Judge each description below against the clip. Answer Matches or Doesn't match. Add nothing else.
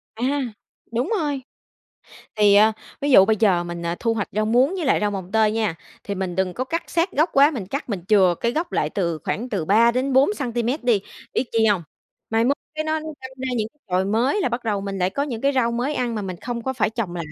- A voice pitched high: Matches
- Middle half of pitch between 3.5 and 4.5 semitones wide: Doesn't match